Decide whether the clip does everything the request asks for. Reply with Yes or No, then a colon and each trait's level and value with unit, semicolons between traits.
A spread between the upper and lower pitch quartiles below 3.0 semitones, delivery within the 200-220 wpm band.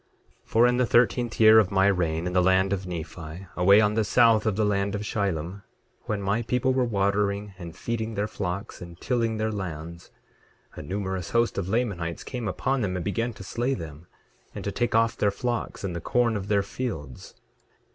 No: average, 3.9 semitones; fast, 205 wpm